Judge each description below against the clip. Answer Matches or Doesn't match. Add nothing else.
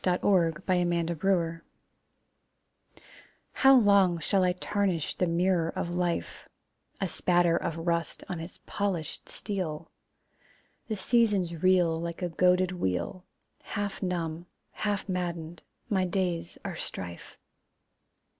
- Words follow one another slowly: Matches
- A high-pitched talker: Doesn't match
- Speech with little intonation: Matches